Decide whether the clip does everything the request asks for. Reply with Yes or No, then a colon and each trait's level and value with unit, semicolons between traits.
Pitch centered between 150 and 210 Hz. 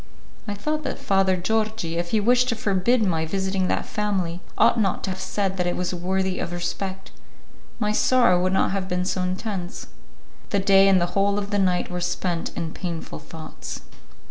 Yes: high, 190 Hz